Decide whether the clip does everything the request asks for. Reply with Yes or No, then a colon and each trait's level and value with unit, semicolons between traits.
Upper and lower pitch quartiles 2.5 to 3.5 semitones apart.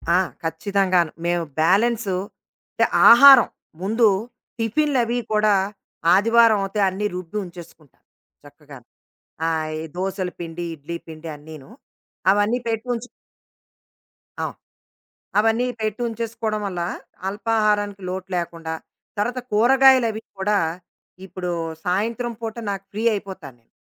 No: average, 4.5 semitones